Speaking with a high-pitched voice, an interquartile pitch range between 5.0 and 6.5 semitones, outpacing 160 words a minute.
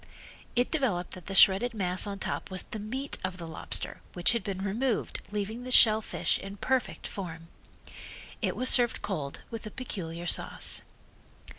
No: high, 200 Hz; average, 4.6 semitones; average, 170 wpm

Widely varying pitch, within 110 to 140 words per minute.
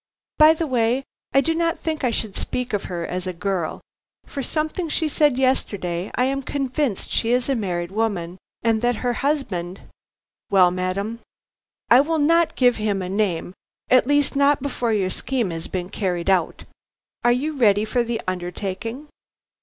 No: wide, 6.6 semitones; average, 175 wpm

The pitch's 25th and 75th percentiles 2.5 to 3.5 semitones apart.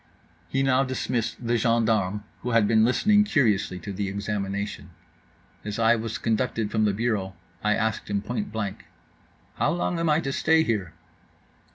Yes: average, 3.2 semitones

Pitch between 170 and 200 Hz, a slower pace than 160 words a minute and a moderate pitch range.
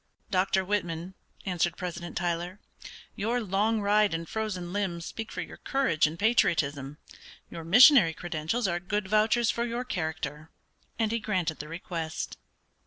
Yes: medium, 185 Hz; average, 145 wpm; average, 4.5 semitones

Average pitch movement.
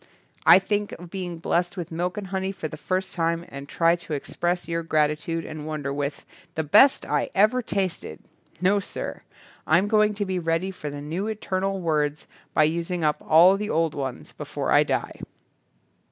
Yes: average, 3.5 semitones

